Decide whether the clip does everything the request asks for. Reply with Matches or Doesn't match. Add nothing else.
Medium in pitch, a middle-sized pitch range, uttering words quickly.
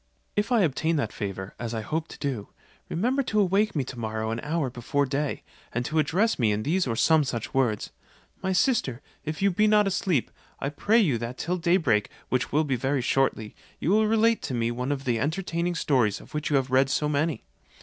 Doesn't match